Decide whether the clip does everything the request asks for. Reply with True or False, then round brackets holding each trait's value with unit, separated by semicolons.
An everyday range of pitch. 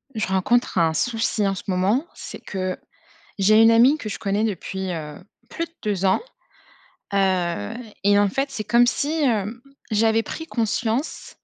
True (3.6 semitones)